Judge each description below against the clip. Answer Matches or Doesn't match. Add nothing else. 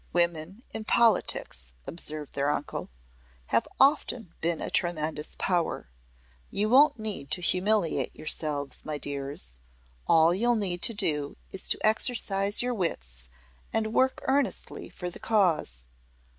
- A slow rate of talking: Matches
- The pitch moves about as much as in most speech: Doesn't match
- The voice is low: Doesn't match